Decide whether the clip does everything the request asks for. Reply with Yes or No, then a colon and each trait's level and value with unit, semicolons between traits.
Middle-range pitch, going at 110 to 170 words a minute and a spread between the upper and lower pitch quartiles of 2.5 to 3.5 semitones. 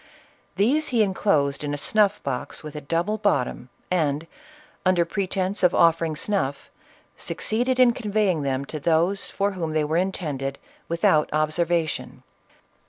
No: medium, 170 Hz; average, 150 wpm; average, 5.0 semitones